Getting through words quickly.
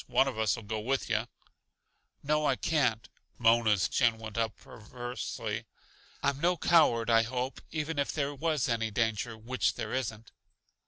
No: average, 155 wpm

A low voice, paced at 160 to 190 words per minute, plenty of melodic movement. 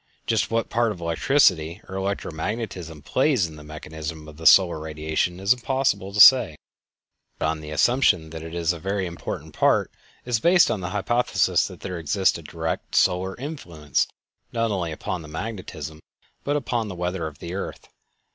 Yes: very low, 90 Hz; average, 175 wpm; wide, 5.8 semitones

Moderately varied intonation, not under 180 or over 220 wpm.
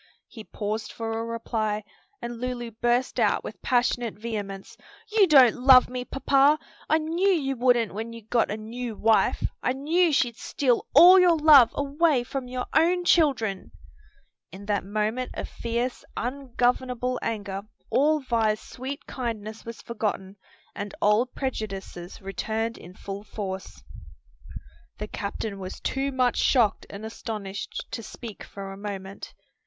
No: average, 3.7 semitones; average, 145 wpm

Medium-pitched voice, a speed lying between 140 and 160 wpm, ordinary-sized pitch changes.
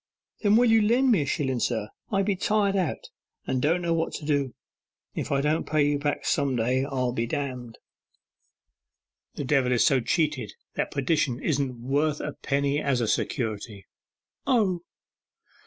No: medium, 145 Hz; average, 170 wpm; average, 4.6 semitones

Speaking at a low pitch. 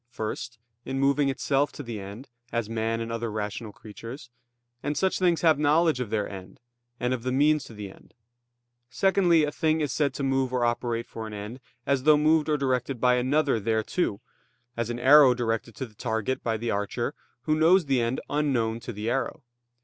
Yes: low, 125 Hz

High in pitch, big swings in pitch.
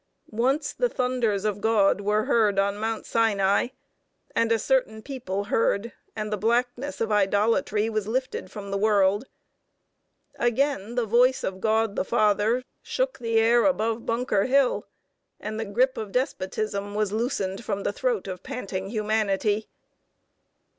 No: high, 220 Hz; average, 3.0 semitones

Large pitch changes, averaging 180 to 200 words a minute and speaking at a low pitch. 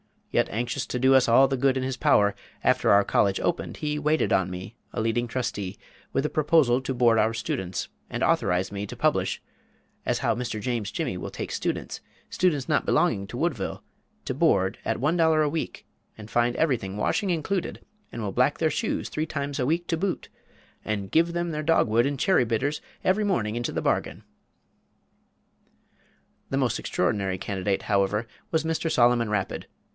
Yes: wide, 6.5 semitones; average, 190 wpm; low, 125 Hz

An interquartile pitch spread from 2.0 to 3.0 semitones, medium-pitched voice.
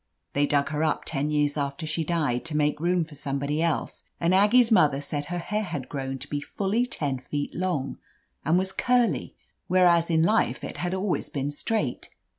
No: average, 4.0 semitones; medium, 155 Hz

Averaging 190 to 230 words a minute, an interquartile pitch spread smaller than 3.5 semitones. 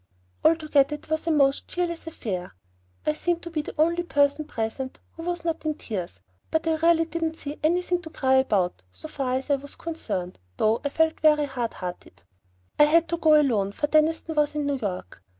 No: fast, 205 wpm; average, 3.8 semitones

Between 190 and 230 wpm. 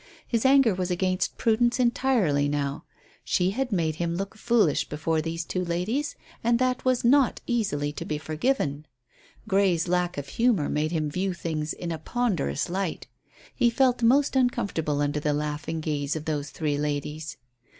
No: average, 165 wpm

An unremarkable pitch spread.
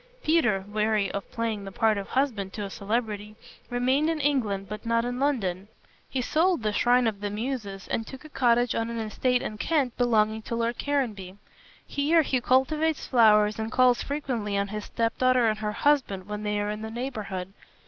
Yes: average, 3.5 semitones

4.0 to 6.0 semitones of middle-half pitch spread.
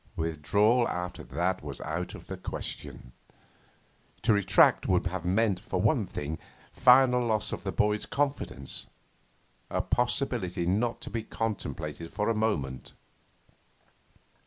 Yes: average, 5.1 semitones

